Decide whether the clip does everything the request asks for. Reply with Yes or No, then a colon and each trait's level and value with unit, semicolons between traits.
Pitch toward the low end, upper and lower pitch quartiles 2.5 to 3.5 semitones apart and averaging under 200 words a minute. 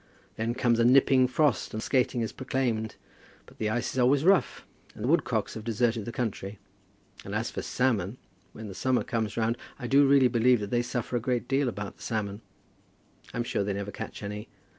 No: low, 120 Hz; average, 2.9 semitones; fast, 205 wpm